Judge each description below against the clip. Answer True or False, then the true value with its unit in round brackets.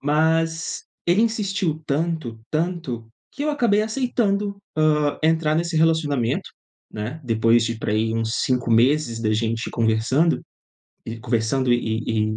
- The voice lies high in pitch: False (145 Hz)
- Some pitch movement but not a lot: False (6.5 semitones)